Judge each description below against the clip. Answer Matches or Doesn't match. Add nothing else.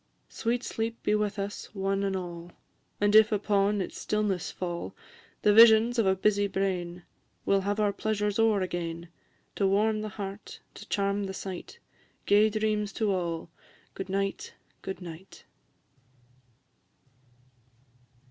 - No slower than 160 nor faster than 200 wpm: Doesn't match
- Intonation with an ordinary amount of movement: Doesn't match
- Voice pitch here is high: Matches